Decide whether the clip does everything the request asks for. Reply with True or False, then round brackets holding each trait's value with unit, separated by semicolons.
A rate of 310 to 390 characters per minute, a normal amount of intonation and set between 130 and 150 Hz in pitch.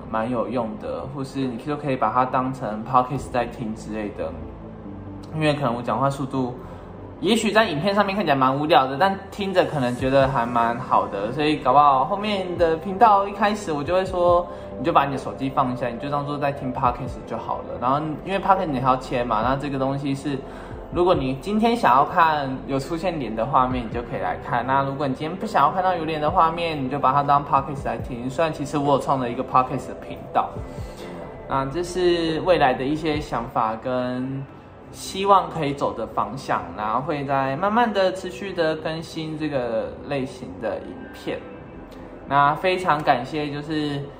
True (325 characters per minute; 4.5 semitones; 140 Hz)